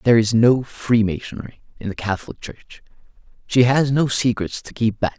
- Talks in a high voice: No, low, 115 Hz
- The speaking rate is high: No, average, 175 wpm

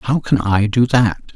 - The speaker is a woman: No, male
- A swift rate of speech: Yes, fast, 220 wpm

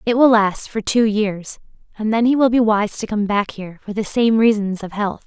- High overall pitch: Yes, high, 215 Hz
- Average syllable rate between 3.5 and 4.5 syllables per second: No, 5.1 syllables/s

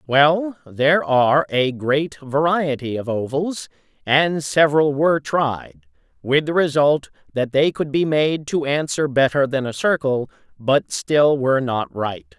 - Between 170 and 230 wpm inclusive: No, average, 150 wpm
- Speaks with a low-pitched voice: No, medium, 145 Hz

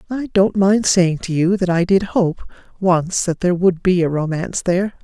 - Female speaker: Yes, female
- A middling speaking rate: No, fast, 215 wpm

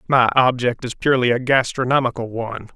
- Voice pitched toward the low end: Yes, low, 125 Hz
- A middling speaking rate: Yes, average, 150 wpm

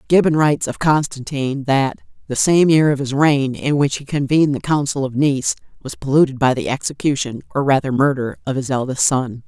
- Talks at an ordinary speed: Yes, average, 195 wpm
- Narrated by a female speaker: Yes, female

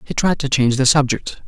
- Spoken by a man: Yes, male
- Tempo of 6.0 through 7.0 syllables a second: Yes, 6.3 syllables/s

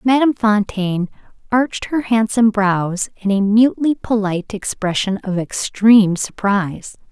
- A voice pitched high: Yes, high, 210 Hz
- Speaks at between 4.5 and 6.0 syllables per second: Yes, 4.9 syllables/s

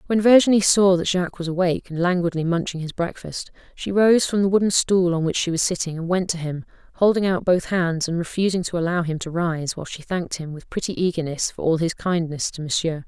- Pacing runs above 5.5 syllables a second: Yes, 5.9 syllables/s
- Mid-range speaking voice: Yes, medium, 175 Hz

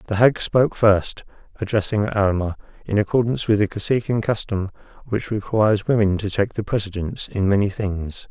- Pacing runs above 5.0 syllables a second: Yes, 5.5 syllables/s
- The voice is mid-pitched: No, low, 105 Hz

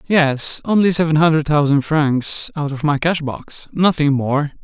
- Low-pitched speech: No, medium, 150 Hz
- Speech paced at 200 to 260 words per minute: No, average, 155 wpm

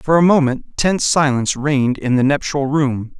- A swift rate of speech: No, average, 190 wpm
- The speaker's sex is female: No, male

